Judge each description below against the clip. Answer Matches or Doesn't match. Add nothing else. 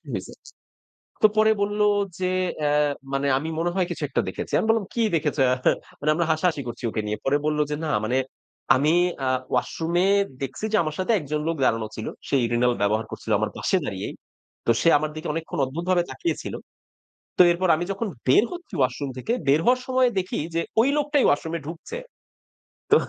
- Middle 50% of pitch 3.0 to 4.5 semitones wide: Doesn't match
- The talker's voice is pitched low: Doesn't match